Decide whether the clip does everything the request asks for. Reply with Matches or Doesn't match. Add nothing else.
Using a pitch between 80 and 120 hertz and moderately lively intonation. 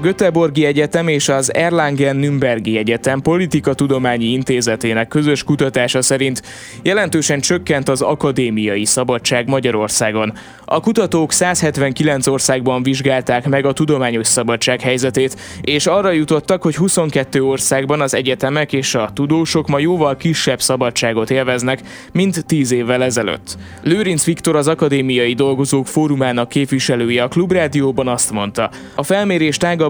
Doesn't match